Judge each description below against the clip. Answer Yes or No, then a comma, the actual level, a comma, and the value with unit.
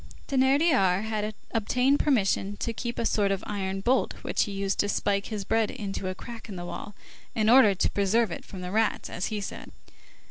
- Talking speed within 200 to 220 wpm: Yes, fast, 205 wpm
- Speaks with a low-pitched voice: No, high, 210 Hz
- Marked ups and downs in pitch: No, average, 3.0 semitones